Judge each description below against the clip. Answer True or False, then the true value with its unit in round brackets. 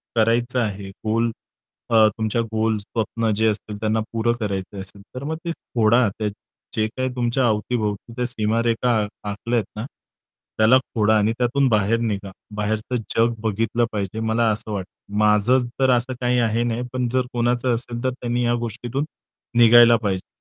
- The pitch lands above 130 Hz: False (115 Hz)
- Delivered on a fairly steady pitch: True (2.1 semitones)